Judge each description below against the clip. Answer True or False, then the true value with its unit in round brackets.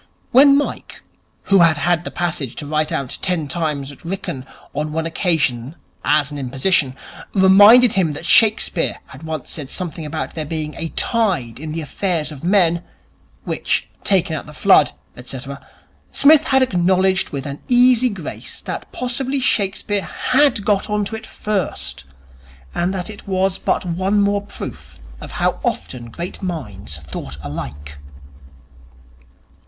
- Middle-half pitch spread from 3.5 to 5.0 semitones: False (5.5 semitones)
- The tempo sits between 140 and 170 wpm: True (150 wpm)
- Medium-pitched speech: True (170 Hz)